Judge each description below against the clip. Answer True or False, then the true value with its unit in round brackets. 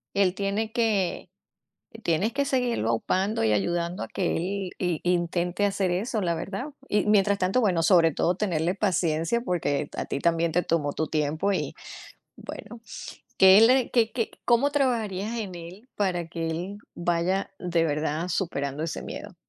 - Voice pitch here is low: False (185 Hz)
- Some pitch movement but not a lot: True (3.9 semitones)